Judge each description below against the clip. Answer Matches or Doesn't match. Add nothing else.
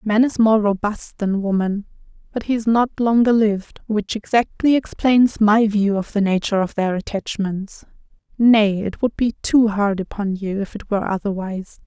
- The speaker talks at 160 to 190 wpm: Matches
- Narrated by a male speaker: Doesn't match